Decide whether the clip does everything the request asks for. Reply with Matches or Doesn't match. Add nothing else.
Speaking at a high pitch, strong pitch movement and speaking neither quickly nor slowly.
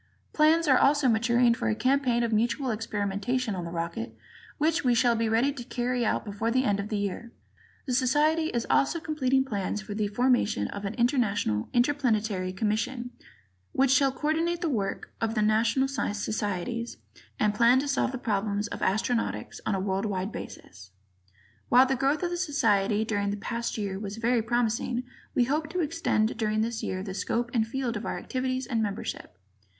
Doesn't match